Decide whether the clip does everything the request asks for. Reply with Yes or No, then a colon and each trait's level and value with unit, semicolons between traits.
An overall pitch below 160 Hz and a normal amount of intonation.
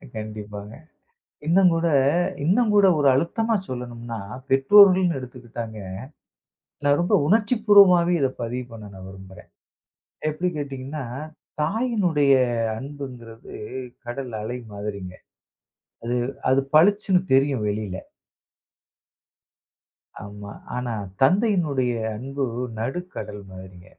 No: low, 135 Hz; wide, 7.8 semitones